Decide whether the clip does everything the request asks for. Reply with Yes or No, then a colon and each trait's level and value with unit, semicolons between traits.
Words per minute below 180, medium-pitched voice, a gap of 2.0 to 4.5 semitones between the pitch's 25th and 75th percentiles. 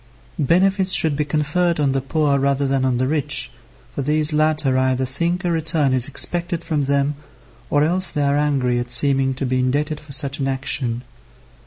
No: average, 190 wpm; medium, 145 Hz; narrow, 2.6 semitones